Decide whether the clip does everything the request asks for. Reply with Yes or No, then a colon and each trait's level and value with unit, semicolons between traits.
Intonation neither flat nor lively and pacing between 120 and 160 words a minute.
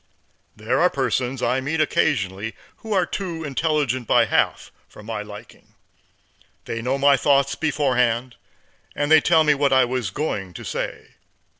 Yes: average, 4.4 semitones; average, 150 wpm